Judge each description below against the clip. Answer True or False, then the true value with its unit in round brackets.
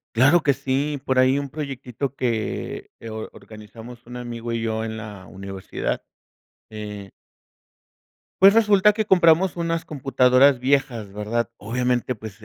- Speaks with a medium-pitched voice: False (125 Hz)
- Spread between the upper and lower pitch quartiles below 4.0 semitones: False (4.3 semitones)